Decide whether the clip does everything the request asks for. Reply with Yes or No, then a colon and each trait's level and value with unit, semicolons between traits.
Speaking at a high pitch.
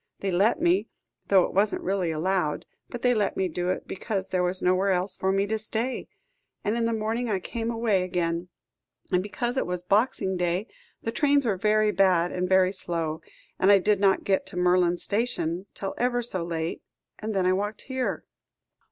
Yes: high, 195 Hz